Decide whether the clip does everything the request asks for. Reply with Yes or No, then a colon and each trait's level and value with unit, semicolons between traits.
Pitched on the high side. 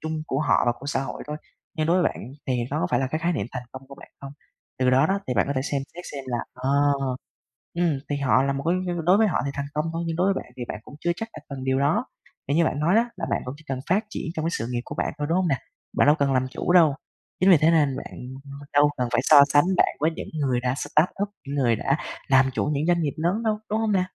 No: medium, 145 Hz